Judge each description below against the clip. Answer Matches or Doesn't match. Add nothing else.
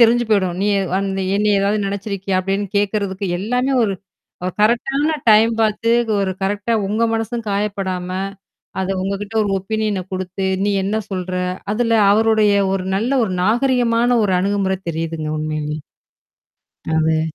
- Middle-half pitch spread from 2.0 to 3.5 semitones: Matches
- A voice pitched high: Matches